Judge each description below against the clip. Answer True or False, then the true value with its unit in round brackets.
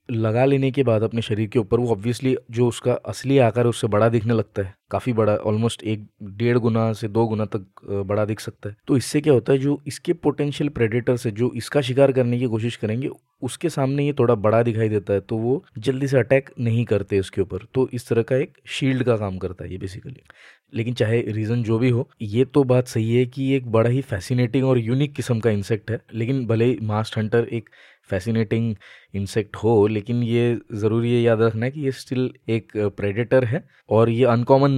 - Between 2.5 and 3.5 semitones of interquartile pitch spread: True (2.8 semitones)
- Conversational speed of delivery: False (215 wpm)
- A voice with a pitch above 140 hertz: False (120 Hz)